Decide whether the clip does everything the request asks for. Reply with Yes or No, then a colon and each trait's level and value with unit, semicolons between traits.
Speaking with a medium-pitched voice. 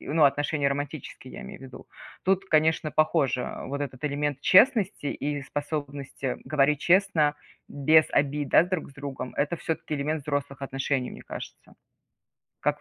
Yes: medium, 145 Hz